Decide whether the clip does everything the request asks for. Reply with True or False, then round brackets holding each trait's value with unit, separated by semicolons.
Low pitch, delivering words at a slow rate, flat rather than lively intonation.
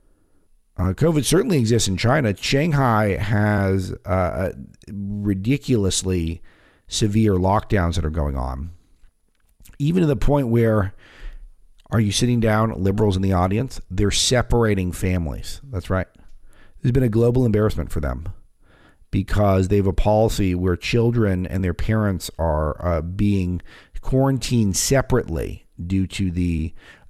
False (100 Hz; 130 wpm; 4.1 semitones)